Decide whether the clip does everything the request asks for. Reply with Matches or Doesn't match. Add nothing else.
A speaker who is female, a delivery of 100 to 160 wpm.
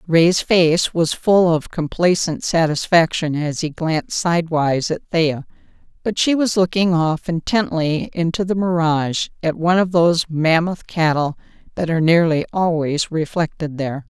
Matches